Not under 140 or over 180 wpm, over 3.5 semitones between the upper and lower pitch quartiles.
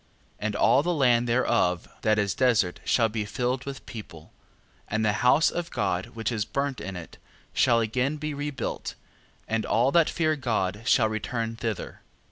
Yes: average, 175 wpm; average, 3.9 semitones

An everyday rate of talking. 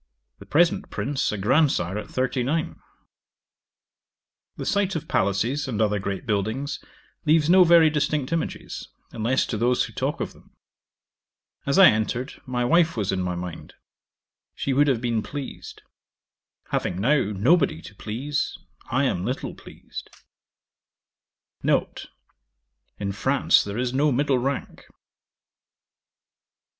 No: slow, 130 wpm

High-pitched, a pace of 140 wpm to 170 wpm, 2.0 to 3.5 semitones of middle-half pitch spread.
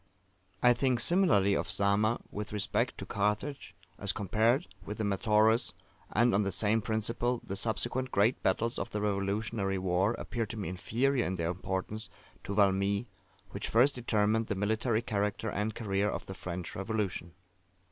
No: low, 105 Hz; average, 160 wpm; average, 2.7 semitones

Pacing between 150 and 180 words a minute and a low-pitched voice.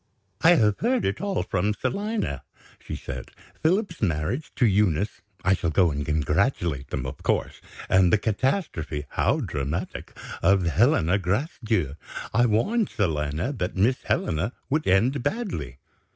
No: average, 140 wpm; low, 100 Hz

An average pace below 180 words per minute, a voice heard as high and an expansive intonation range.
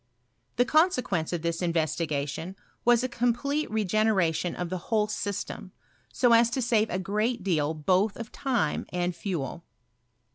Yes: average, 145 wpm; high, 200 Hz; wide, 5.7 semitones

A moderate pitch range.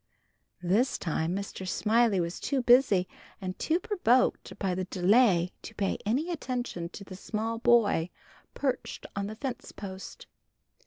Yes: average, 4.9 semitones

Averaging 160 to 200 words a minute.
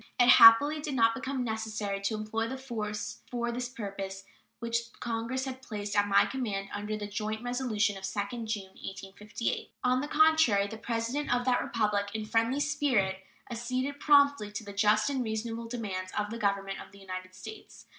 Yes: average, 185 wpm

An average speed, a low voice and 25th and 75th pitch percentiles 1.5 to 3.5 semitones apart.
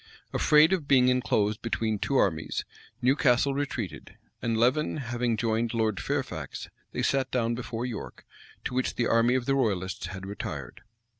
Yes: average, 160 wpm; low, 120 Hz; average, 3.0 semitones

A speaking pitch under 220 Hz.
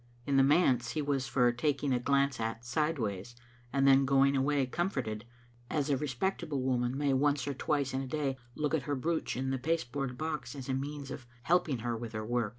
Yes: low, 135 Hz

